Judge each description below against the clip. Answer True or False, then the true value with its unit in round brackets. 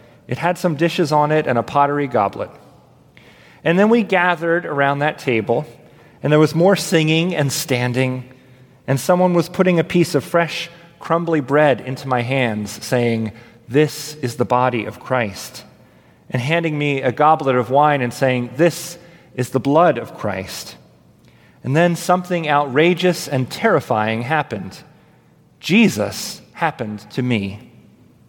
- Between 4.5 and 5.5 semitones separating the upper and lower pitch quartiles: True (5.1 semitones)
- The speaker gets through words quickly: False (150 wpm)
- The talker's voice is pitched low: False (145 Hz)